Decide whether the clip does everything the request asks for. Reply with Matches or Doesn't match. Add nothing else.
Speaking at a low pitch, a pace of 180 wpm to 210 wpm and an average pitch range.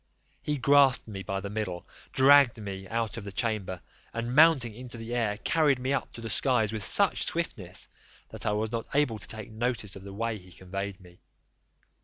Matches